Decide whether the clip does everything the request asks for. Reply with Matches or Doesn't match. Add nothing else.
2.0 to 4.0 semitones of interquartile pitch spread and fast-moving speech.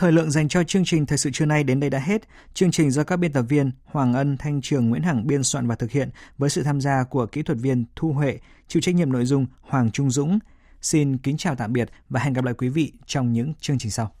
Matches